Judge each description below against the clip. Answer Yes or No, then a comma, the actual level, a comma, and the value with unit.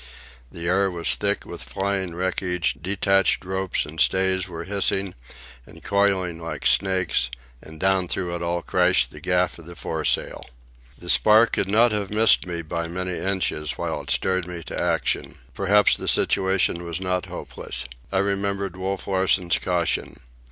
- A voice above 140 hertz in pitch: No, very low, 95 Hz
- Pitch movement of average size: No, narrow, 2.1 semitones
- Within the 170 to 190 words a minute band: No, average, 160 wpm